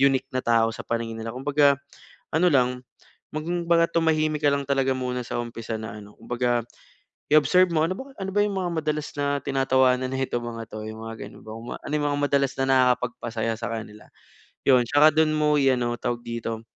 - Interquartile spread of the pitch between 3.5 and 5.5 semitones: Yes, average, 4.4 semitones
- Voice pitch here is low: Yes, low, 130 Hz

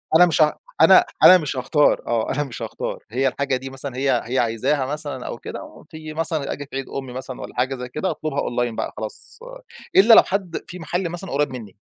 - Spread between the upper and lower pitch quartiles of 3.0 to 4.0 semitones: Yes, average, 3.7 semitones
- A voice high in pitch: No, medium, 140 Hz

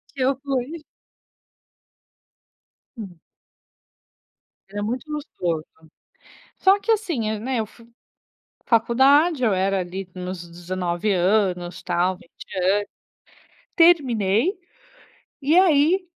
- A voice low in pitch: No, high, 220 Hz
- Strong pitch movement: Yes, wide, 7.8 semitones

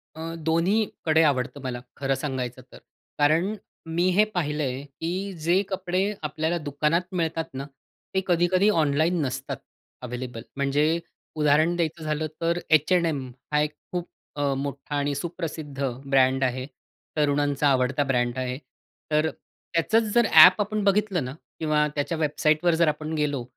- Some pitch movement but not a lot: Yes, average, 3.5 semitones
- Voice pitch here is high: No, medium, 155 Hz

